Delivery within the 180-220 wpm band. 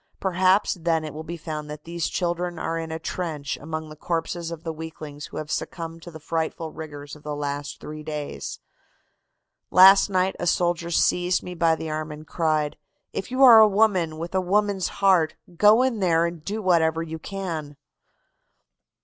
Yes: average, 185 wpm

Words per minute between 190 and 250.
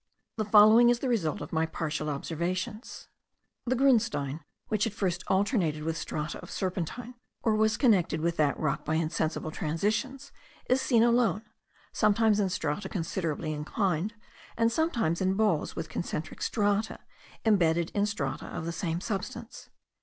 No: average, 150 wpm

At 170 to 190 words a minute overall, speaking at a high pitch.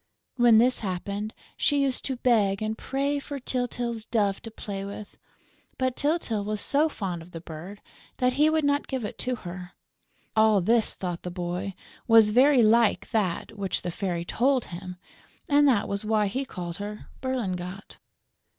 Yes: average, 175 wpm; high, 215 Hz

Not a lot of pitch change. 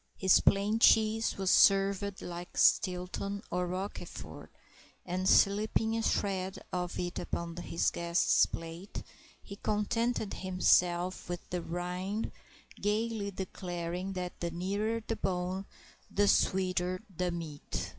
Yes: narrow, 2.2 semitones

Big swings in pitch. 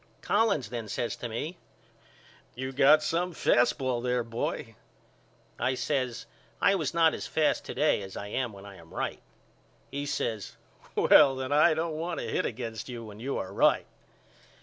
No: average, 5.0 semitones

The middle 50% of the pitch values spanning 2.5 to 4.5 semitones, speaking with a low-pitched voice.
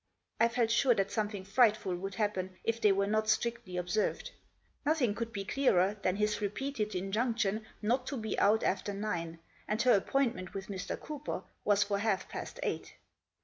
No: average, 3.0 semitones; high, 210 Hz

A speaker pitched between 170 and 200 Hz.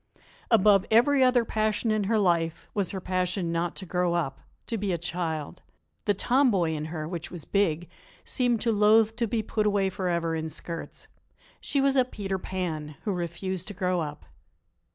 Yes: high, 190 Hz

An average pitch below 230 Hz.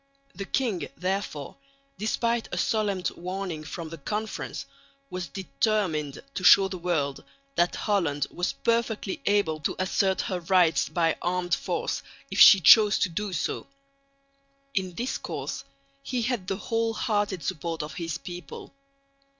Yes: medium, 185 Hz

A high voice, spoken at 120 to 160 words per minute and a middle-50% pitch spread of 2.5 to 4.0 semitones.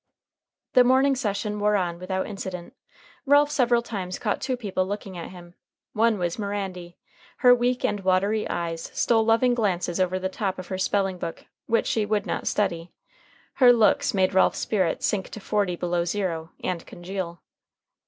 No: high, 195 Hz; average, 170 wpm; average, 3.5 semitones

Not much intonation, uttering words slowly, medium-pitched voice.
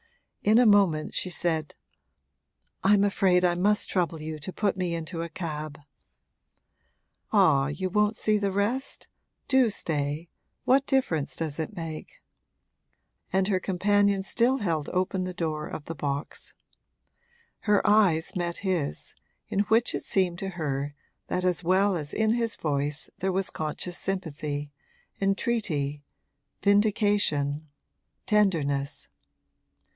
No: average, 4.7 semitones; slow, 130 wpm; medium, 180 Hz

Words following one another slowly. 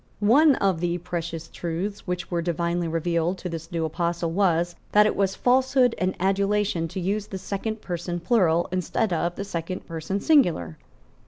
No: average, 170 wpm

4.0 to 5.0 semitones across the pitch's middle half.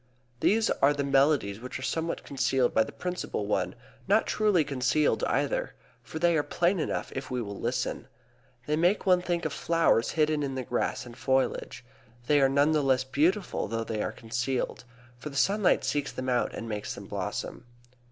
Yes: average, 4.6 semitones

